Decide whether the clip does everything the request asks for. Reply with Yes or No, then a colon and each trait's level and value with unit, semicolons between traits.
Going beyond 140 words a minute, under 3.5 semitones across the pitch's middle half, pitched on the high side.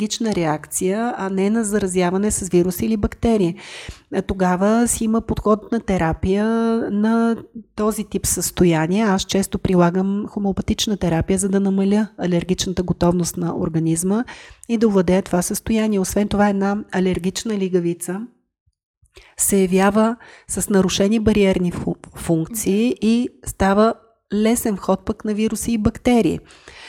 No: average, 125 wpm; average, 3.1 semitones; high, 200 Hz